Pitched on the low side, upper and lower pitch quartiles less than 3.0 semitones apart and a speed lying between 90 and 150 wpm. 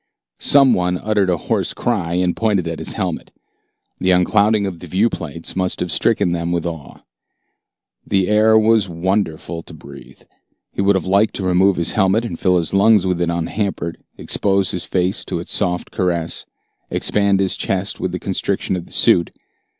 No: very low, 95 Hz; narrow, 2.6 semitones; average, 180 wpm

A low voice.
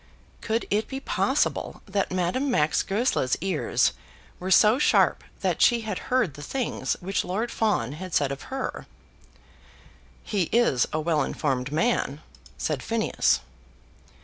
No: high, 190 Hz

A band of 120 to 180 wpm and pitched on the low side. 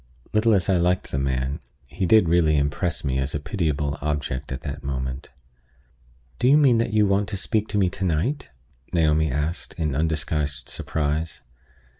Yes: average, 175 wpm; very low, 80 Hz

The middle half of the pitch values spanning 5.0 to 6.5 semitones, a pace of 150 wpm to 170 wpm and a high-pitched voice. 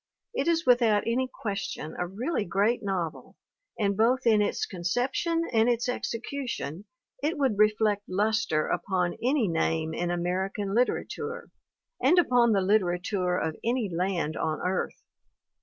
No: average, 5.3 semitones; average, 140 wpm; high, 210 Hz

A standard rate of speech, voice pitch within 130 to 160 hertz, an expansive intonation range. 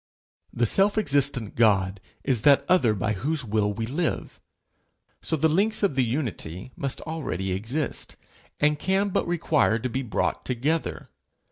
Yes: average, 150 wpm; low, 135 Hz; wide, 6.4 semitones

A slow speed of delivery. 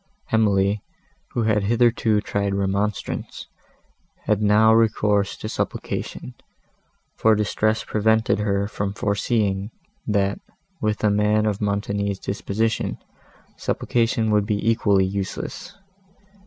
Yes: slow, 105 wpm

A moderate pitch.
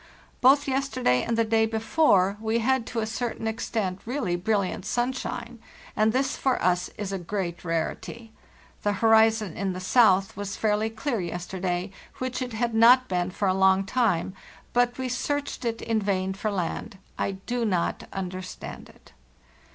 No: high, 220 Hz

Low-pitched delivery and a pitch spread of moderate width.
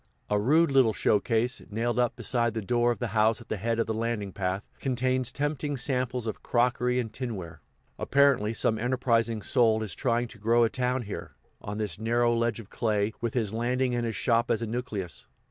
No: low, 115 Hz; narrow, 2.2 semitones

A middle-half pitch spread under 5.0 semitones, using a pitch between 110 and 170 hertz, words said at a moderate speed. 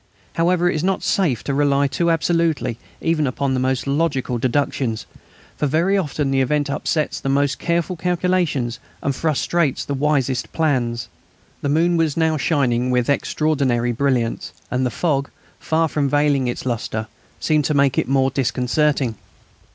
Yes: average, 3.6 semitones; medium, 140 Hz; average, 160 wpm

